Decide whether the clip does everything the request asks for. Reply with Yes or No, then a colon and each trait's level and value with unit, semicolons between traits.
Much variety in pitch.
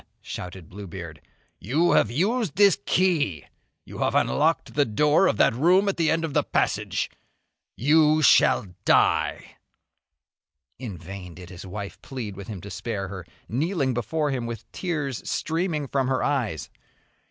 Yes: wide, 8.3 semitones